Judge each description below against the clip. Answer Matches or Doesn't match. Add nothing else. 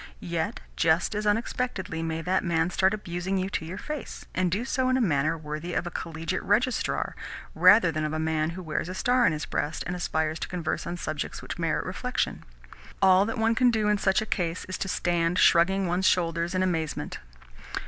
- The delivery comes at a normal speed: Doesn't match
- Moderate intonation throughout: Matches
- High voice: Doesn't match